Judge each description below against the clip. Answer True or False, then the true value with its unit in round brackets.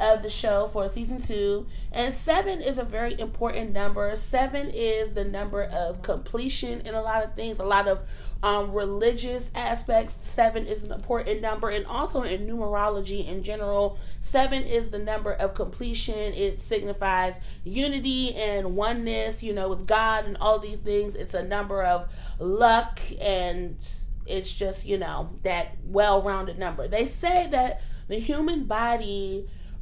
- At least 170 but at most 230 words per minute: False (160 wpm)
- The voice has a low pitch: False (210 Hz)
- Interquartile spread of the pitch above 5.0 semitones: False (2.6 semitones)